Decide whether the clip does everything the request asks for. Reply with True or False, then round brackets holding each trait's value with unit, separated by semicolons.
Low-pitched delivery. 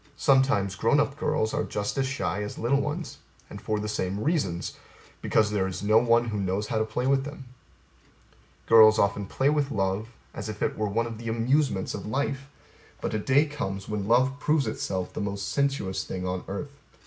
True (110 Hz)